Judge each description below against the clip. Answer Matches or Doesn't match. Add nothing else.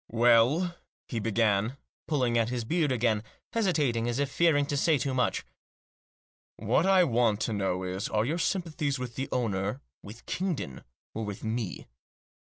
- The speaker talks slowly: Doesn't match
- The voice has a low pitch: Matches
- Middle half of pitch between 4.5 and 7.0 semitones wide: Matches